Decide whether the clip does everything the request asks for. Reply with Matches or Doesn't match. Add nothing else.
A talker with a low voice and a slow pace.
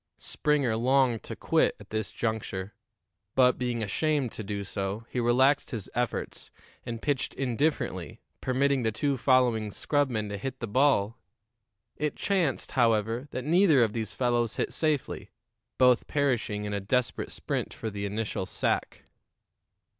Doesn't match